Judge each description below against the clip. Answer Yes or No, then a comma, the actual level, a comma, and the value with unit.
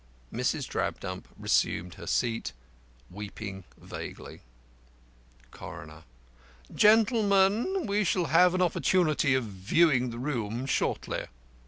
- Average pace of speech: No, slow, 105 wpm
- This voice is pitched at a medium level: Yes, medium, 145 Hz